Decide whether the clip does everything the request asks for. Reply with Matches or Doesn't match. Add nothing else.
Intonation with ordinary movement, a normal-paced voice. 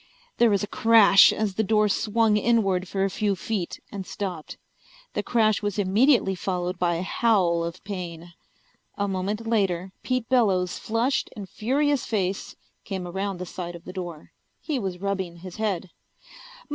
Matches